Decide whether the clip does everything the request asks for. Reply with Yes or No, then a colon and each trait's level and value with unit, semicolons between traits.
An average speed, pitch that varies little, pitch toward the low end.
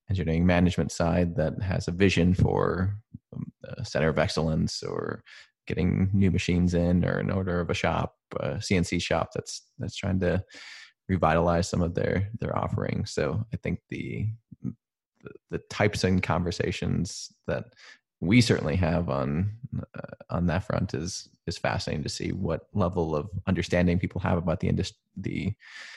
No: average, 160 wpm; average, 3.2 semitones; very low, 90 Hz